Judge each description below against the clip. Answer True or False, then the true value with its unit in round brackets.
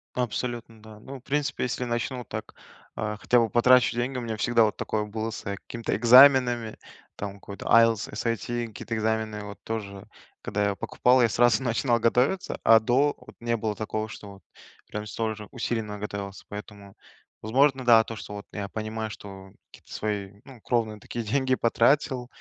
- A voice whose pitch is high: False (115 Hz)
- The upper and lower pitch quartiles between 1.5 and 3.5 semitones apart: True (2.4 semitones)